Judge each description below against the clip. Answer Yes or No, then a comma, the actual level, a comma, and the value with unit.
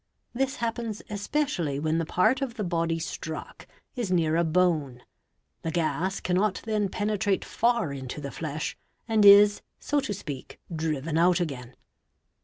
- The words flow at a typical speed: Yes, average, 150 wpm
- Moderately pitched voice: Yes, medium, 180 Hz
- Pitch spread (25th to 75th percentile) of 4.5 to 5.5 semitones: Yes, average, 5.2 semitones